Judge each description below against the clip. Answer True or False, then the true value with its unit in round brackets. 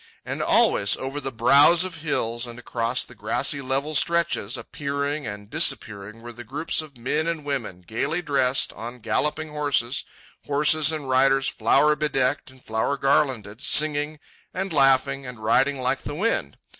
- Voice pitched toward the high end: False (135 Hz)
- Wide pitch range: False (4.0 semitones)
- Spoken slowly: False (155 wpm)